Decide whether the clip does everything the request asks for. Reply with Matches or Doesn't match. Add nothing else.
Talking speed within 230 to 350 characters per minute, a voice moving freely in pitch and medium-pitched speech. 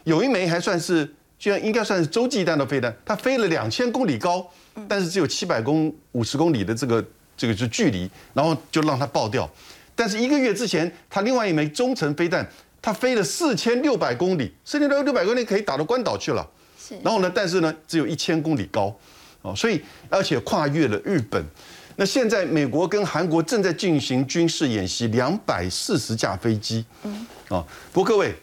Matches